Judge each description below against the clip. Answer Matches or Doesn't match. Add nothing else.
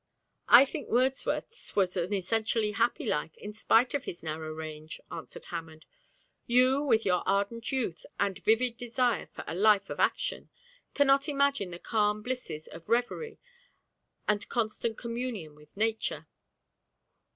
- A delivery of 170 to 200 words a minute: Doesn't match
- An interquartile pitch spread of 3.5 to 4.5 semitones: Doesn't match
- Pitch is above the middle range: Matches